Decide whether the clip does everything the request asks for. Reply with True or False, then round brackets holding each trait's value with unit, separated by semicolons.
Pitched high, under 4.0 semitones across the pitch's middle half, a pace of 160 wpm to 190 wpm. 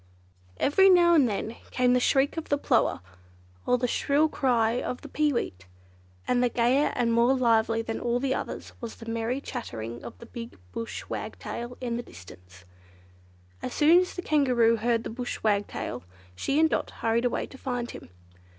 True (240 Hz; 3.1 semitones; 175 wpm)